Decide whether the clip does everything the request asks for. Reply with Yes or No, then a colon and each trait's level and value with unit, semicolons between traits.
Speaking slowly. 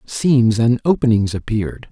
Yes: slow, 125 wpm